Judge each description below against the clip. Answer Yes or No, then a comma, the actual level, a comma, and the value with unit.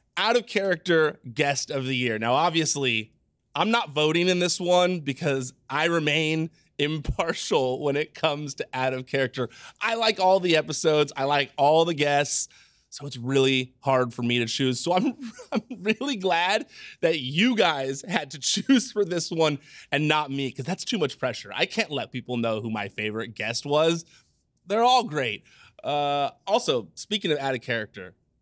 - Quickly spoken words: No, average, 180 wpm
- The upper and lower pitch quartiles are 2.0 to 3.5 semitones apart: No, wide, 5.4 semitones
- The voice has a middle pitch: Yes, medium, 145 Hz